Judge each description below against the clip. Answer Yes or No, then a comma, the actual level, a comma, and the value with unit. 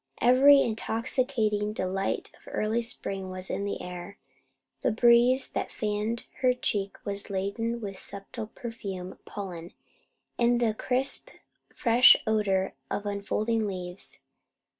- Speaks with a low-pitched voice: No, high, 215 Hz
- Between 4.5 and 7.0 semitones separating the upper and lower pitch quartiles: No, average, 3.2 semitones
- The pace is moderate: No, slow, 125 wpm